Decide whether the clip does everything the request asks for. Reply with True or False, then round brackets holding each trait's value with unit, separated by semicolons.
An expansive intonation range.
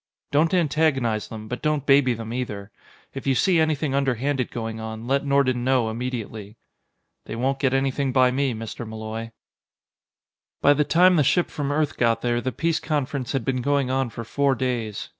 False (3.5 semitones)